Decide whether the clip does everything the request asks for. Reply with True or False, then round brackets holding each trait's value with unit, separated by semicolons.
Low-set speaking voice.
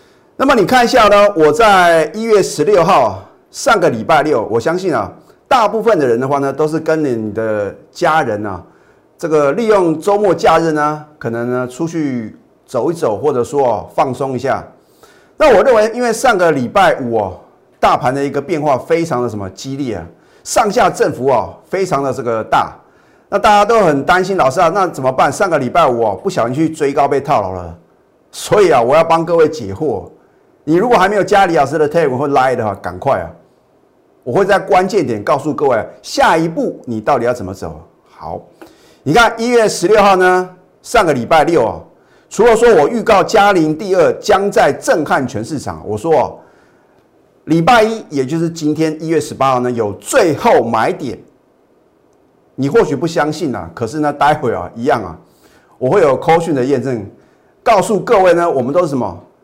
False (155 Hz)